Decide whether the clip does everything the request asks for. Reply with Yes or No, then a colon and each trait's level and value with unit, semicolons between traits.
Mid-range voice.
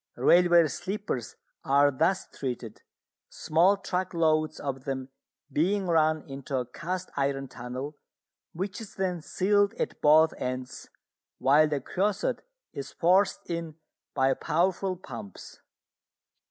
Yes: medium, 155 Hz